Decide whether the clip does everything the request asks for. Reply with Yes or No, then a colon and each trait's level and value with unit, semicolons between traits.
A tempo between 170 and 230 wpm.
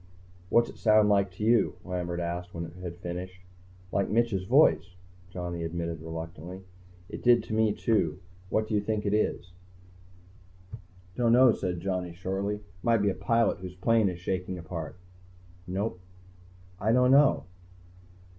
No: average, 155 wpm